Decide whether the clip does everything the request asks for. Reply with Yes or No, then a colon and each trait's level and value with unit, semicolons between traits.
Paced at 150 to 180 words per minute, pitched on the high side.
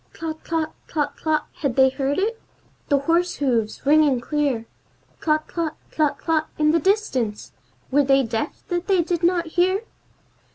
Yes: average, 160 wpm; very high, 310 Hz